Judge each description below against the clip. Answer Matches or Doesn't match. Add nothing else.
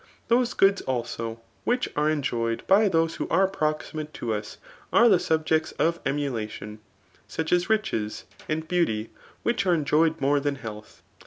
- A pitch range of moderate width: Doesn't match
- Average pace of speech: Matches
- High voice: Doesn't match